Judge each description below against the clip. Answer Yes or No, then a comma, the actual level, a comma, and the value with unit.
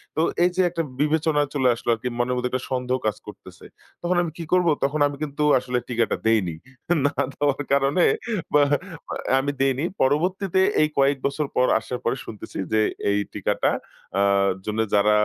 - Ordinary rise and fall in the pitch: Yes, average, 3.6 semitones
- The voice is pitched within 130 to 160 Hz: Yes, medium, 140 Hz